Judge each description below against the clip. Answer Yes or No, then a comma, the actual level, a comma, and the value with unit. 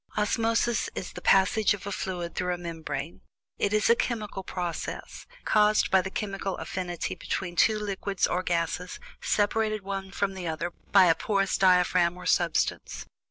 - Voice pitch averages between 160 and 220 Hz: Yes, high, 190 Hz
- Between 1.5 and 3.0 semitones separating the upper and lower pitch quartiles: Yes, average, 2.7 semitones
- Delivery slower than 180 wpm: Yes, average, 160 wpm